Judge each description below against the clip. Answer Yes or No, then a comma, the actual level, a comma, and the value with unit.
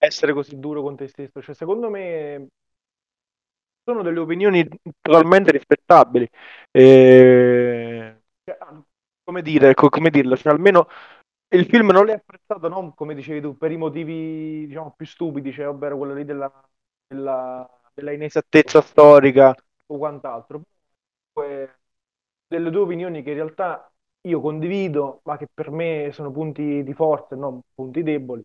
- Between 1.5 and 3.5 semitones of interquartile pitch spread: Yes, average, 3.1 semitones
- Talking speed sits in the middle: Yes, average, 145 wpm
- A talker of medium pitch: Yes, medium, 150 Hz